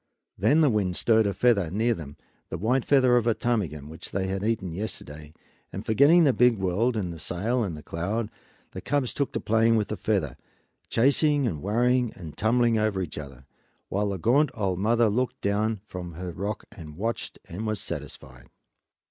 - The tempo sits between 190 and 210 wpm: Yes, average, 195 wpm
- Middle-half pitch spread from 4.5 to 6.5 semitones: Yes, average, 4.9 semitones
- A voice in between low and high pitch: No, low, 105 Hz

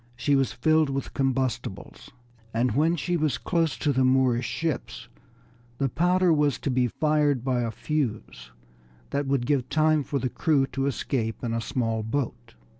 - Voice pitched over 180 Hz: No, low, 135 Hz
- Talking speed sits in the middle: Yes, average, 170 wpm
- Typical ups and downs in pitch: Yes, average, 3.7 semitones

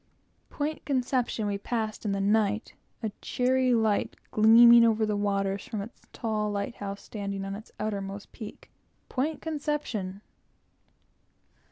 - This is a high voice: Yes, high, 215 Hz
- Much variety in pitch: No, average, 3.1 semitones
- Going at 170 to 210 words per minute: No, slow, 135 wpm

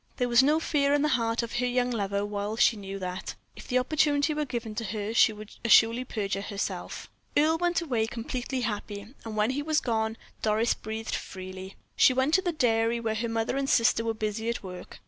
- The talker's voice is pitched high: Yes, high, 230 Hz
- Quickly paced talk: Yes, fast, 215 wpm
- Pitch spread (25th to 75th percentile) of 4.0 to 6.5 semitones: No, average, 3.4 semitones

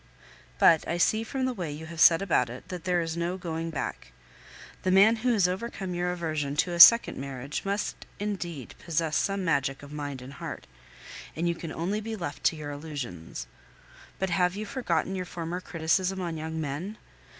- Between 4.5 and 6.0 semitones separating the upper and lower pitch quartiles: No, average, 3.9 semitones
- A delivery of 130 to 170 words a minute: No, average, 195 wpm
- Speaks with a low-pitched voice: No, medium, 170 Hz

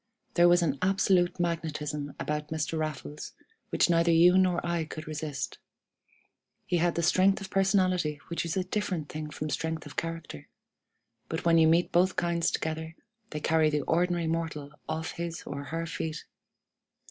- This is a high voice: No, medium, 165 Hz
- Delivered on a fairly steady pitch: Yes, narrow, 2.1 semitones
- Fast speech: No, average, 165 wpm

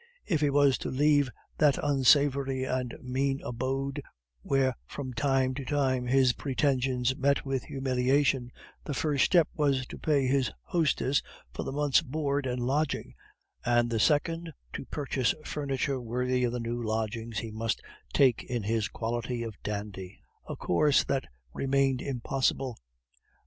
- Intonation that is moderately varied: No, narrow, 2.3 semitones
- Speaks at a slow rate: No, average, 150 wpm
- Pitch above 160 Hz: No, low, 130 Hz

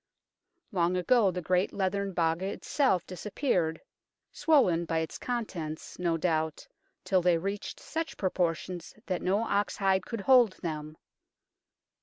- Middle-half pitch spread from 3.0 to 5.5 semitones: Yes, average, 3.3 semitones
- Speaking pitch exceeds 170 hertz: Yes, medium, 185 Hz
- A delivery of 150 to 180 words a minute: No, slow, 135 wpm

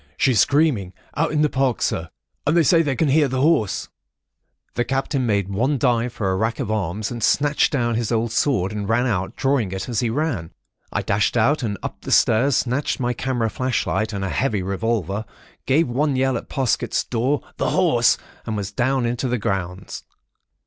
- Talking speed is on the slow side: No, average, 195 wpm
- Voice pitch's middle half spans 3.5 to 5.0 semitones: Yes, average, 4.4 semitones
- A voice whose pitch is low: Yes, low, 120 Hz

